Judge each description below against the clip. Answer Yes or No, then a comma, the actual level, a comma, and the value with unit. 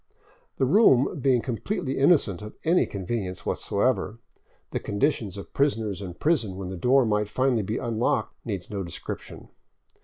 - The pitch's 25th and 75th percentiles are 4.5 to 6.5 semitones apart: Yes, average, 5.1 semitones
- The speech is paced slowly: No, average, 150 wpm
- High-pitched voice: No, low, 110 Hz